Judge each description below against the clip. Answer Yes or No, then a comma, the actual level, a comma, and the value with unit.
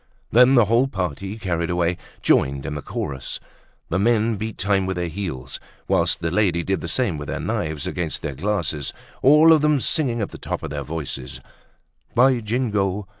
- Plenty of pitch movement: Yes, wide, 6.0 semitones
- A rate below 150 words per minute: No, average, 185 wpm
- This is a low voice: Yes, very low, 95 Hz